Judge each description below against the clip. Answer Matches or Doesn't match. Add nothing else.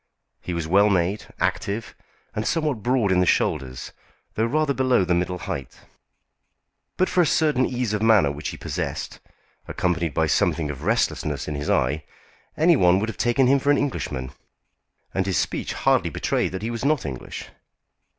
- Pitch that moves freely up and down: Matches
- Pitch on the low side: Matches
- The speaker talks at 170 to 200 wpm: Matches